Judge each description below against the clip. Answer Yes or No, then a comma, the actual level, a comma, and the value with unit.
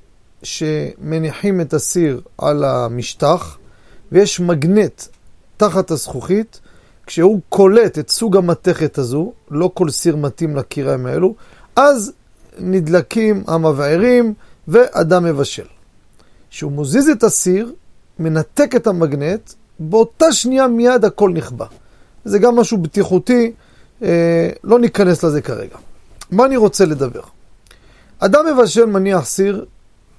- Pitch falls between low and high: Yes, medium, 180 Hz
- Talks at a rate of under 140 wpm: Yes, average, 105 wpm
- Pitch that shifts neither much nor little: No, wide, 6.1 semitones